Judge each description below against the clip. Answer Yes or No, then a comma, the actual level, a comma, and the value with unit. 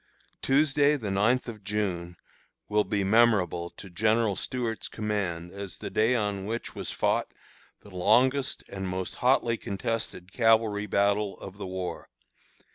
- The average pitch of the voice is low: Yes, low, 105 Hz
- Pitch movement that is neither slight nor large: Yes, average, 3.1 semitones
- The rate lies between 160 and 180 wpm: No, average, 140 wpm